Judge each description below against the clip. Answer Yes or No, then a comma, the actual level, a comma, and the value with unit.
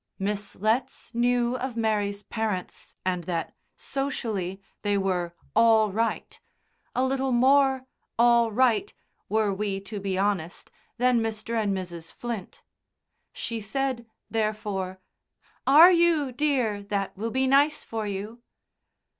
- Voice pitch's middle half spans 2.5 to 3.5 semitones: No, average, 4.0 semitones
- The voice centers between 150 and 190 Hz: No, high, 220 Hz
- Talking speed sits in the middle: No, slow, 125 wpm